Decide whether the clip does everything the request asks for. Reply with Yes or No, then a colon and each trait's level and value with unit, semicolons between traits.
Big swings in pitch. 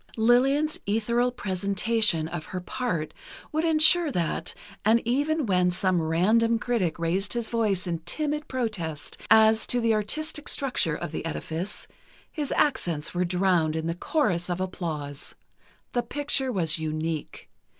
Yes: wide, 6.5 semitones